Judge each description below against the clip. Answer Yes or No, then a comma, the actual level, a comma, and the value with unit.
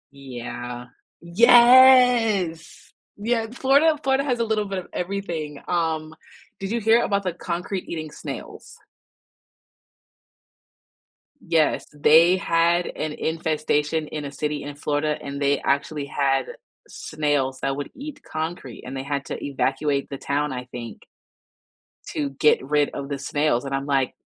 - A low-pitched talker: No, medium, 155 Hz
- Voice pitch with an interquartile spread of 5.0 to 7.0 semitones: Yes, wide, 5.5 semitones